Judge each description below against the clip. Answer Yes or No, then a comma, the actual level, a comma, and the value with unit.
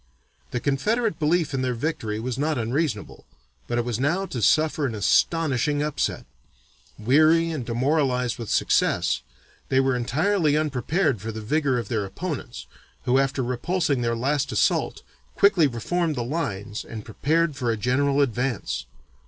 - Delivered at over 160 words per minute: No, average, 155 wpm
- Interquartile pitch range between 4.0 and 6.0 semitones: Yes, average, 4.7 semitones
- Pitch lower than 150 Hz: Yes, low, 135 Hz